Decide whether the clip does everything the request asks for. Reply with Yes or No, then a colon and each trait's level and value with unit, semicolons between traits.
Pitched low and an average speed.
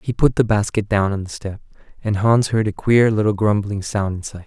No: low, 105 Hz; fast, 230 wpm